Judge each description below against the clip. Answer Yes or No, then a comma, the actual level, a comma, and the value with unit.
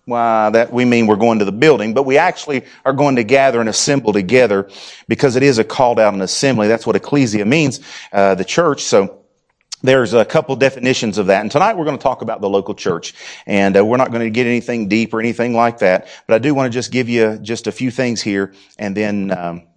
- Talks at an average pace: No, fast, 260 wpm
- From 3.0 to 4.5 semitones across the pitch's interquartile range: Yes, average, 3.7 semitones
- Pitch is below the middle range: Yes, low, 115 Hz